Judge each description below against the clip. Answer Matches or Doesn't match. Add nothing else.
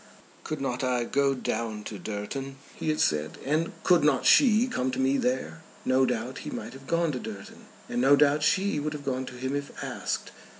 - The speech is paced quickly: Matches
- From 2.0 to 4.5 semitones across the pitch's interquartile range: Matches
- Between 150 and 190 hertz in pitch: Doesn't match